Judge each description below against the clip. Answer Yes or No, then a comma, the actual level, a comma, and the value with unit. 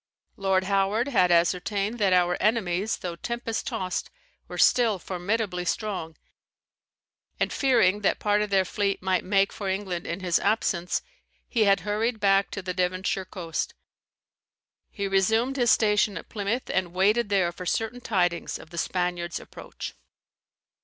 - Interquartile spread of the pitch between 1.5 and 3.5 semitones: Yes, average, 2.9 semitones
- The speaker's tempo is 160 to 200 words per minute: No, average, 150 wpm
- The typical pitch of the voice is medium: No, high, 195 Hz